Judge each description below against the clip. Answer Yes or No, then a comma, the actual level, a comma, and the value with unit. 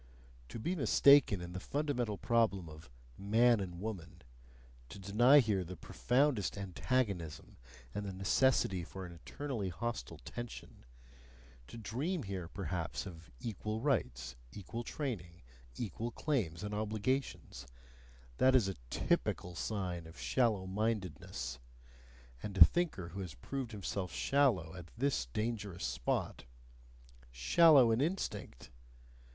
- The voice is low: Yes, low, 100 Hz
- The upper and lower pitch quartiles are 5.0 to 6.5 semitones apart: Yes, wide, 5.4 semitones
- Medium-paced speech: No, slow, 125 wpm